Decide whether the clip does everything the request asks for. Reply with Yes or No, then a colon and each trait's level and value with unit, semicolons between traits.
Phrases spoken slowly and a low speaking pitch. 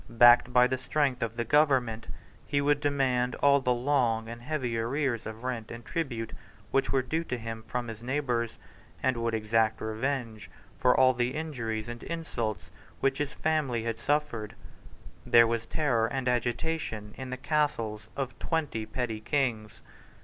No: average, 165 wpm; low, 125 Hz